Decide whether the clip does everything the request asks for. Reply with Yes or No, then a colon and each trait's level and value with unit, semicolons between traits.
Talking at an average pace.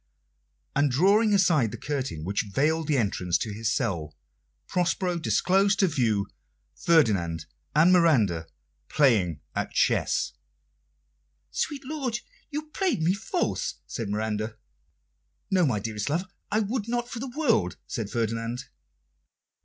No: slow, 130 wpm